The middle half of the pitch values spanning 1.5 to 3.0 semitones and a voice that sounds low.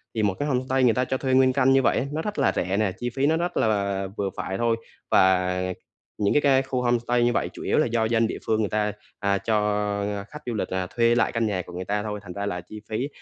No: average, 4.2 semitones; low, 115 Hz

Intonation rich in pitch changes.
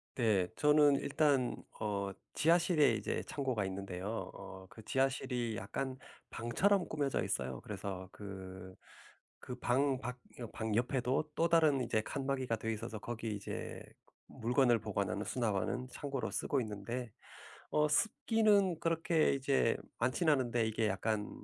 No: average, 4.9 semitones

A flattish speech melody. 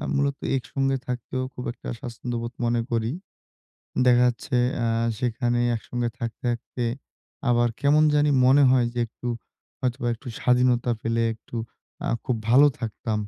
Yes: narrow, 1.7 semitones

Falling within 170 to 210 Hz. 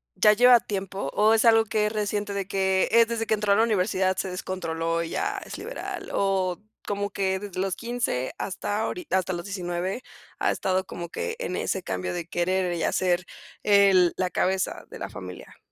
Yes: high, 190 Hz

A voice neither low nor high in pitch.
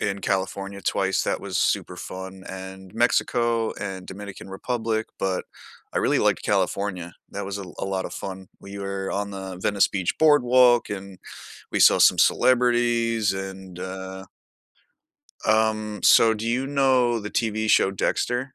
No: low, 100 Hz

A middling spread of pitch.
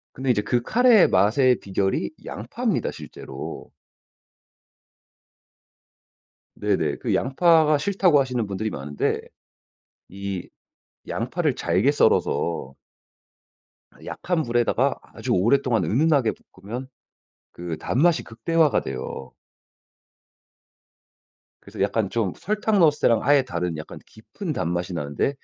No: wide, 7.8 semitones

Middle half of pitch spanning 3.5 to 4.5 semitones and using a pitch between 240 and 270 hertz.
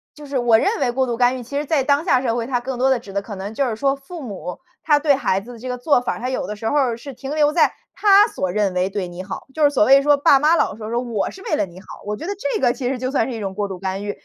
No: average, 5.2 semitones; very high, 250 Hz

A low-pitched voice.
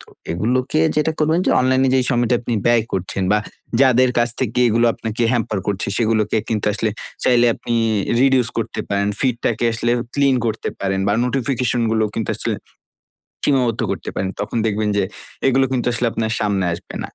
Yes: low, 120 Hz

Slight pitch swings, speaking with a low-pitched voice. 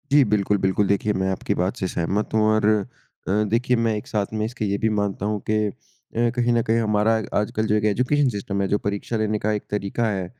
Yes: narrow, 2.0 semitones; low, 105 Hz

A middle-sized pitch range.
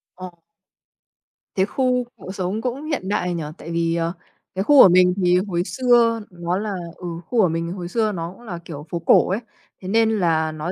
Yes: average, 4.5 semitones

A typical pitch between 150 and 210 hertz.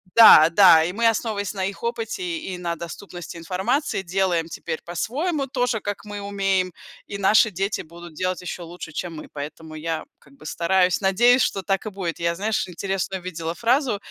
Yes: high, 190 Hz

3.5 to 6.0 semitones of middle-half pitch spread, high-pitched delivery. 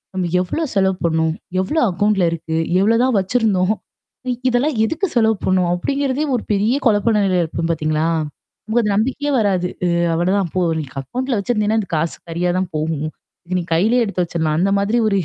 Yes: average, 5.0 semitones; high, 195 Hz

